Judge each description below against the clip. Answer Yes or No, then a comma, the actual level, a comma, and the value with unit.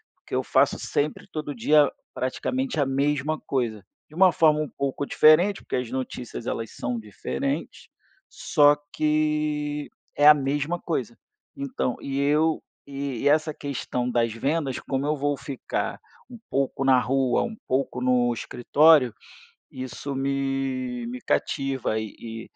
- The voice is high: No, medium, 140 Hz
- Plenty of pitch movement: No, average, 3.1 semitones